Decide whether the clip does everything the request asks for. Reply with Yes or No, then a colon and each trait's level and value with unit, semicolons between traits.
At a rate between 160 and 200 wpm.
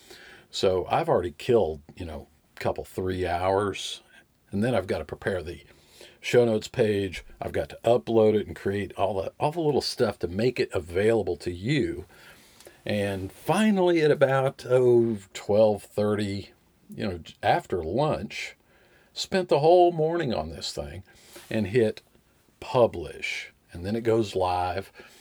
No: average, 150 wpm